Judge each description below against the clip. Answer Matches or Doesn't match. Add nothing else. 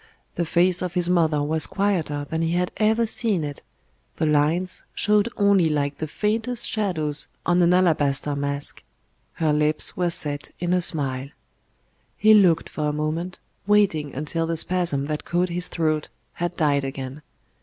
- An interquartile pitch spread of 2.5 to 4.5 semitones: Matches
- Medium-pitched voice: Matches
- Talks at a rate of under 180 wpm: Matches